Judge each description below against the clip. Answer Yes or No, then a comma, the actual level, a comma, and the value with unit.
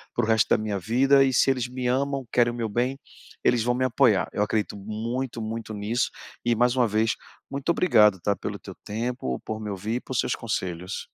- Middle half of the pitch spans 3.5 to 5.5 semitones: No, average, 2.8 semitones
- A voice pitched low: Yes, low, 115 Hz